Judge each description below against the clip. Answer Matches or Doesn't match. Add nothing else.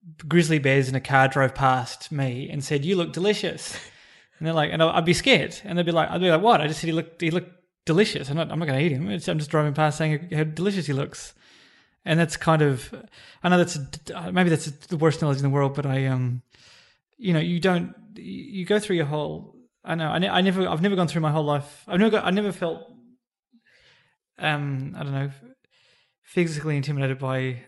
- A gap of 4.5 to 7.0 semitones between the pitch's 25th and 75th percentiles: Doesn't match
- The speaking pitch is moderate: Matches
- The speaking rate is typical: Doesn't match